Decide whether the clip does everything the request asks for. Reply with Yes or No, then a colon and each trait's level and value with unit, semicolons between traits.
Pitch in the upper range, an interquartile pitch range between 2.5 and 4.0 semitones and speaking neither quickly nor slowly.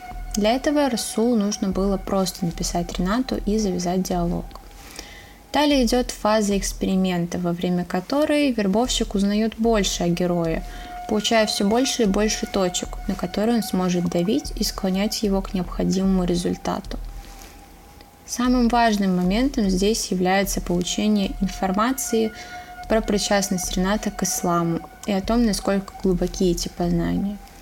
Yes: high, 205 Hz; average, 3.7 semitones; average, 130 wpm